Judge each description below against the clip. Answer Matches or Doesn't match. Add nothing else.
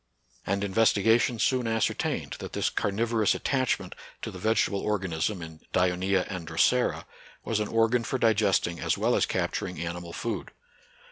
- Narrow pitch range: Doesn't match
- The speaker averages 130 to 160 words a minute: Matches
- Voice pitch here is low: Matches